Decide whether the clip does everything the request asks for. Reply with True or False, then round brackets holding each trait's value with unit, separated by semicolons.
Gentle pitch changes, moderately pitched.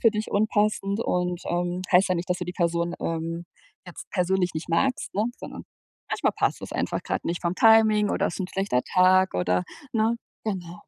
False (3.3 semitones; 180 Hz)